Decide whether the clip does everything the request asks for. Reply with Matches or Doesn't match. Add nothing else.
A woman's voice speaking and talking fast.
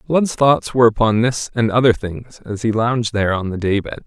Doesn't match